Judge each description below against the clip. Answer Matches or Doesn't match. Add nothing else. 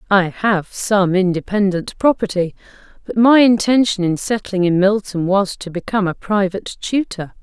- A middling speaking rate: Matches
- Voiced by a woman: Matches